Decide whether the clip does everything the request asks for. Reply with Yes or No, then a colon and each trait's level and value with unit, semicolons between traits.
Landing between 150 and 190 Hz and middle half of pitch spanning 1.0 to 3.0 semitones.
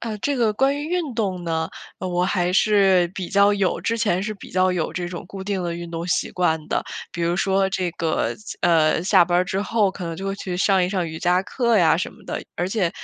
Yes: medium, 185 Hz; narrow, 2.6 semitones